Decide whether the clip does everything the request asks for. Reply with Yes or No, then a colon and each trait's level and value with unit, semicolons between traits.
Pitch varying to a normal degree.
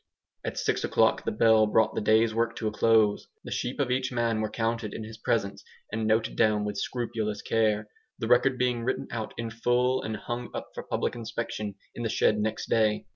No: narrow, 1.6 semitones